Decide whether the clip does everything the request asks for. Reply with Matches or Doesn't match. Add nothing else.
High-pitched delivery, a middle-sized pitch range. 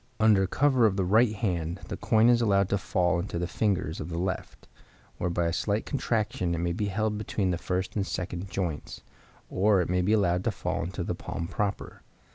Doesn't match